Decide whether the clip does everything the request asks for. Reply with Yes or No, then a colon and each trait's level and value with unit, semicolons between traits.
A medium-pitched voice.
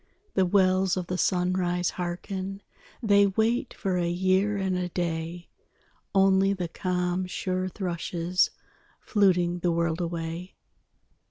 Yes: medium, 180 Hz